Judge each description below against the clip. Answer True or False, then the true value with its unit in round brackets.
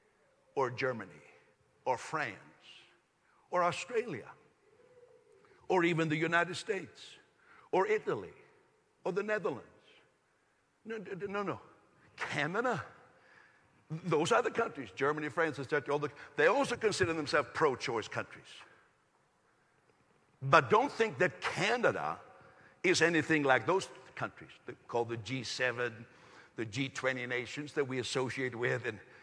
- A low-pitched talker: False (160 Hz)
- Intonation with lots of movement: True (8.2 semitones)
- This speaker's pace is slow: True (120 wpm)